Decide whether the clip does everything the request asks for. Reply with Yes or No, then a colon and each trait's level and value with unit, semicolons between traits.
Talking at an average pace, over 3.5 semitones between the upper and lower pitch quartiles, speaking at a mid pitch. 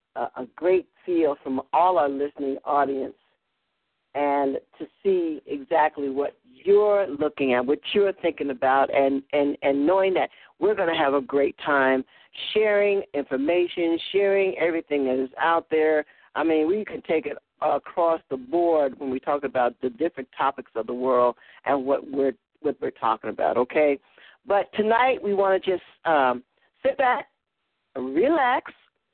Yes: average, 160 wpm; average, 5.2 semitones; medium, 150 Hz